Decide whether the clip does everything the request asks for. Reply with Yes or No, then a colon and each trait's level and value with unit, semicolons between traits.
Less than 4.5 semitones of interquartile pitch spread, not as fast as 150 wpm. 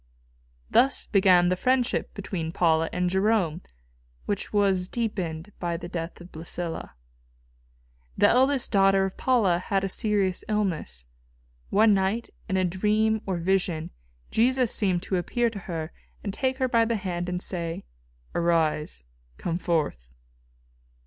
Yes: average, 3.7 semitones; average, 140 wpm